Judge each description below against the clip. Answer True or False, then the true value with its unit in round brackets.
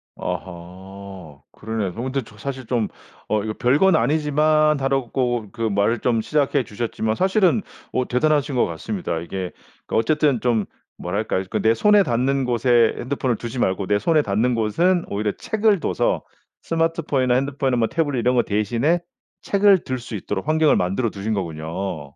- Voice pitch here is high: False (120 Hz)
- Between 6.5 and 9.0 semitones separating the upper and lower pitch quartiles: False (5.9 semitones)